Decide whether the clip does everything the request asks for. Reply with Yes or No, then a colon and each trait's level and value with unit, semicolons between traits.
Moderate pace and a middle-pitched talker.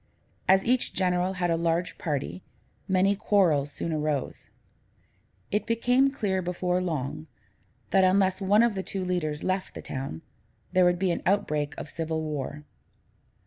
Yes: average, 150 wpm; medium, 180 Hz